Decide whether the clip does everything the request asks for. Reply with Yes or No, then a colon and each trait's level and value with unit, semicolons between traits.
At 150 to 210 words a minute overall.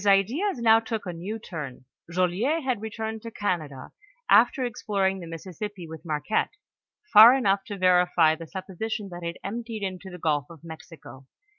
Yes: average, 160 wpm